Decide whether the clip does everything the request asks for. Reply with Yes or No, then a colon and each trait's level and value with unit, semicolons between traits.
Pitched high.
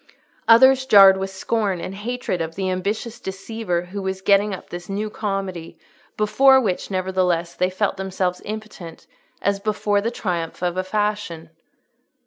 Yes: high, 195 Hz